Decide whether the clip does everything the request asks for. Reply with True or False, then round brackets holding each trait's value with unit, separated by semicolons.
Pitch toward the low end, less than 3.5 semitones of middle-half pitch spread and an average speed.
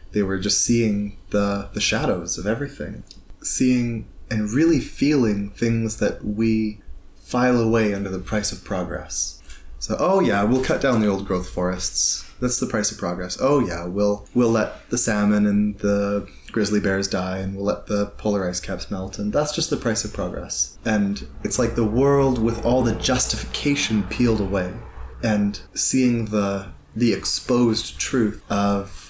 True (105 Hz; 3.1 semitones; 170 wpm)